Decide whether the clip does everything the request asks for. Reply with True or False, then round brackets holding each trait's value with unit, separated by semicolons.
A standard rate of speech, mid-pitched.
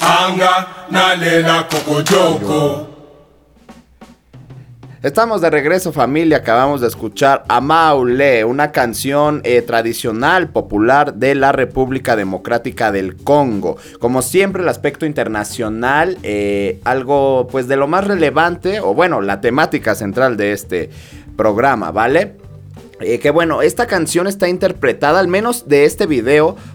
False (115 wpm; 145 Hz)